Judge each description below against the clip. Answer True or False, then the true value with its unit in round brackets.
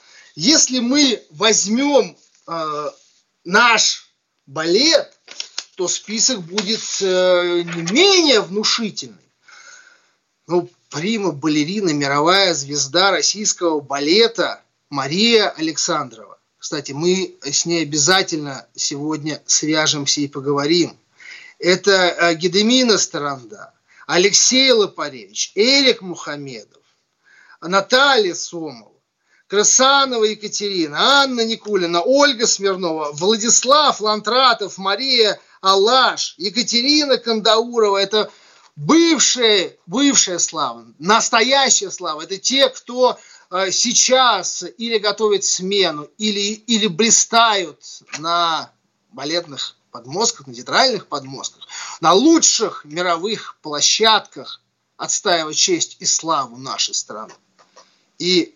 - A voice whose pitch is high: True (200 Hz)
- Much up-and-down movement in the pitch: True (5.9 semitones)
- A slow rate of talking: True (85 wpm)